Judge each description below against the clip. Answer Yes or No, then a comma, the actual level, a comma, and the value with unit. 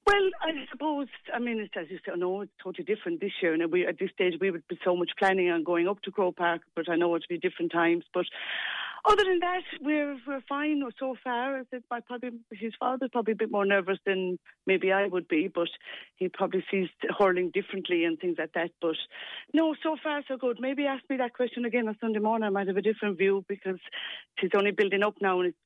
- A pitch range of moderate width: No, wide, 5.7 semitones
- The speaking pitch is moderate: No, high, 200 Hz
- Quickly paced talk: Yes, fast, 235 wpm